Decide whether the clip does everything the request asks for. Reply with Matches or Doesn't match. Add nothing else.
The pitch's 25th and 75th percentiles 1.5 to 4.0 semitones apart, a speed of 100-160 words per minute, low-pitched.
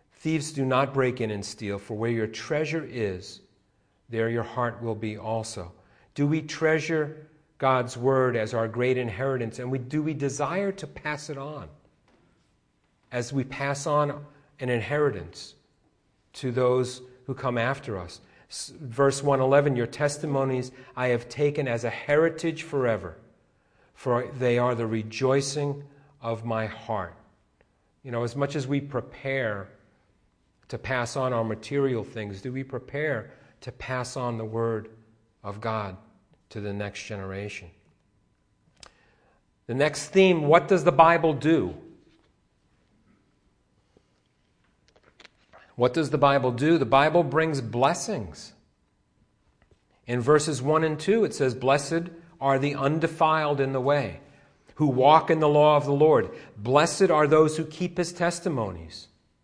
Doesn't match